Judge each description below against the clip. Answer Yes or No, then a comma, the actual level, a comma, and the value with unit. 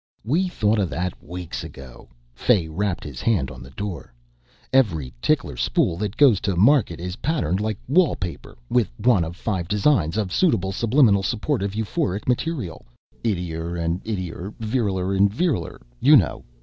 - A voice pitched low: Yes, low, 100 Hz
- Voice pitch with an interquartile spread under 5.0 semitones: No, average, 5.3 semitones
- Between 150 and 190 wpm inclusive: Yes, average, 155 wpm